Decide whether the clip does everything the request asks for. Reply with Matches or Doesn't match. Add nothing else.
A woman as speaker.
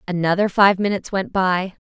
Matches